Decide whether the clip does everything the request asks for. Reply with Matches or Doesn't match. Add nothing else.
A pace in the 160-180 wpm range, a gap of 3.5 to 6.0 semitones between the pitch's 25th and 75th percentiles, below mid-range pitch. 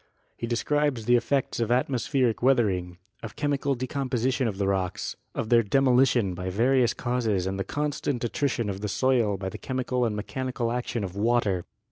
Matches